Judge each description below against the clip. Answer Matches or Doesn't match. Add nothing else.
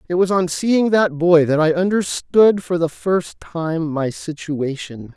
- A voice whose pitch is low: Doesn't match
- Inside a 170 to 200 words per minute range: Matches